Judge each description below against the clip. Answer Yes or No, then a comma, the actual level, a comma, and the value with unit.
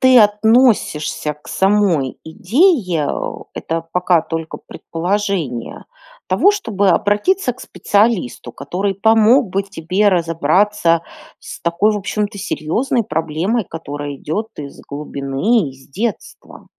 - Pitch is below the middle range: No, high, 190 Hz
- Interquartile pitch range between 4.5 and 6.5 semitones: Yes, average, 5.1 semitones